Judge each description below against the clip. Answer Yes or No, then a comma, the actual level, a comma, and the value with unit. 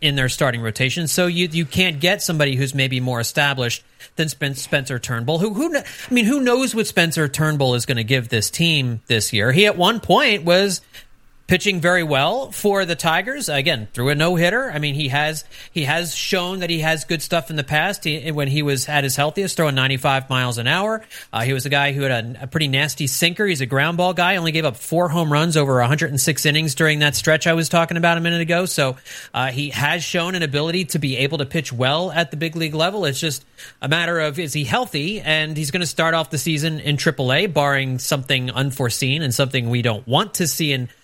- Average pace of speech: No, fast, 235 wpm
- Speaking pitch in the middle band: Yes, medium, 155 Hz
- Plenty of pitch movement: No, average, 4.1 semitones